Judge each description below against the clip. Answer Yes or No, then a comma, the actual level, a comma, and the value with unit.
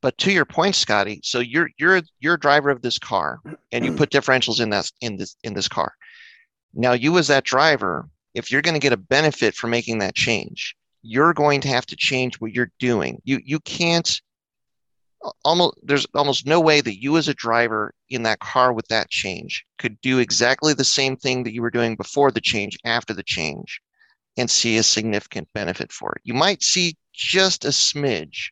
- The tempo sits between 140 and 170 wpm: No, fast, 205 wpm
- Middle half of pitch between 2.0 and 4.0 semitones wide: No, average, 4.5 semitones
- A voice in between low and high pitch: No, low, 130 Hz